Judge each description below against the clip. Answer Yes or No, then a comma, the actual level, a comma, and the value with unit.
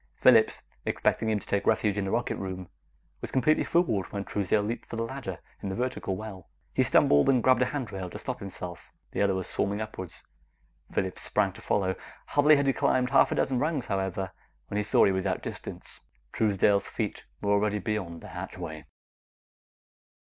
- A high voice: No, low, 105 Hz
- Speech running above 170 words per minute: Yes, average, 190 wpm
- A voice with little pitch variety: No, average, 4.2 semitones